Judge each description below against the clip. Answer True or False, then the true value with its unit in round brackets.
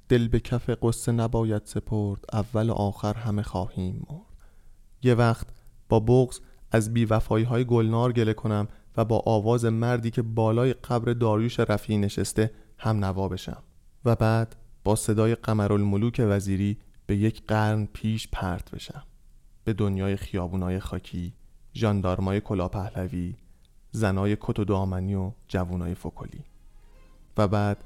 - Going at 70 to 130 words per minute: False (140 wpm)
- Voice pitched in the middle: False (110 Hz)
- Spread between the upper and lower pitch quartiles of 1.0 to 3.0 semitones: True (2.6 semitones)